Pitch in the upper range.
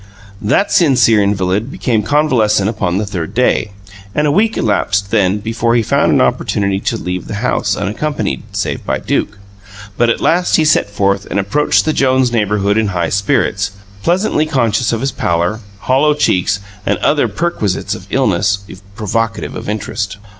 No: low, 105 Hz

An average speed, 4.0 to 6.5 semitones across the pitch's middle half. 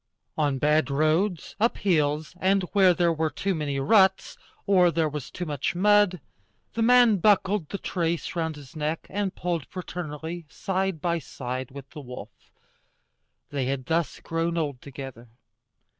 Yes: average, 155 wpm; average, 4.4 semitones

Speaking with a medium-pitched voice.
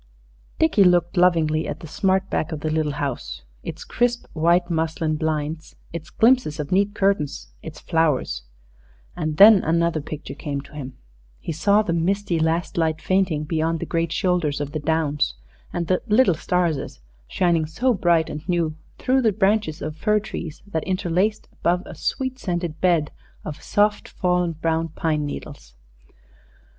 Yes: medium, 165 Hz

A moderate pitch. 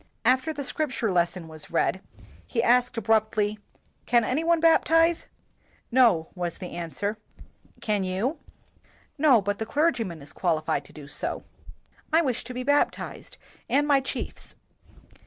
No: high, 225 Hz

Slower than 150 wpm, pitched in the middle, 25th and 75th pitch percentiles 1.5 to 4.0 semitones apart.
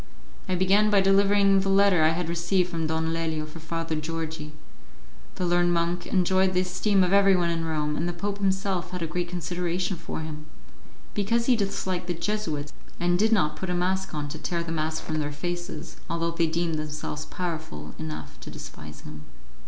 No: average, 190 wpm; medium, 175 Hz; average, 2.9 semitones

